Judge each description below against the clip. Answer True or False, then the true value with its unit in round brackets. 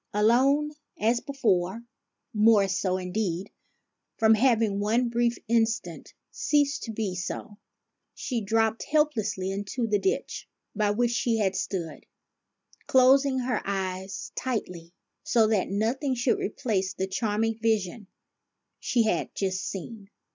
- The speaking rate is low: True (125 wpm)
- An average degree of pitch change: True (3.6 semitones)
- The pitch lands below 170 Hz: False (220 Hz)